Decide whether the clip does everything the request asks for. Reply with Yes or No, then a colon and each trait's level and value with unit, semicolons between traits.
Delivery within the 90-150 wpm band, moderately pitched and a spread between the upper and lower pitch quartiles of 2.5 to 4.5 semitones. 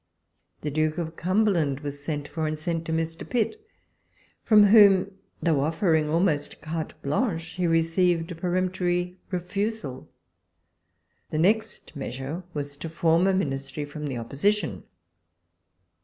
Yes: slow, 135 wpm; medium, 165 Hz; average, 3.5 semitones